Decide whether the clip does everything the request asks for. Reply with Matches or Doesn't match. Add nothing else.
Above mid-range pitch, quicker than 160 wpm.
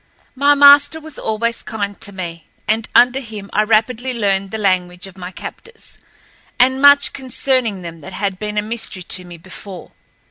Matches